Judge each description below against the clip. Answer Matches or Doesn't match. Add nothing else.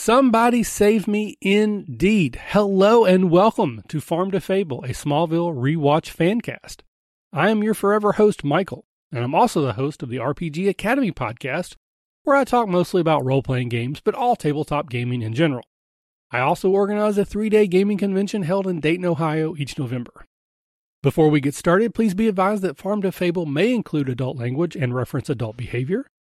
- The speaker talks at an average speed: Matches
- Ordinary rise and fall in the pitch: Doesn't match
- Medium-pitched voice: Matches